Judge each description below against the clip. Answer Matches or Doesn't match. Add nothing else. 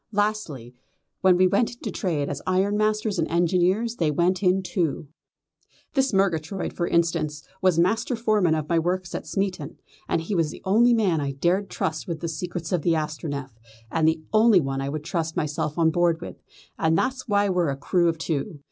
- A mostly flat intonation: Doesn't match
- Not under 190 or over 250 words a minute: Matches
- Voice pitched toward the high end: Doesn't match